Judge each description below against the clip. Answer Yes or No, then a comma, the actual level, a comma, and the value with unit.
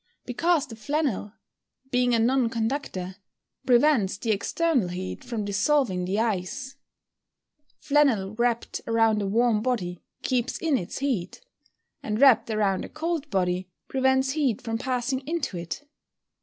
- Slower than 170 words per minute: Yes, average, 140 wpm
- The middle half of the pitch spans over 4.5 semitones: Yes, average, 5.1 semitones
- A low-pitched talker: No, high, 235 Hz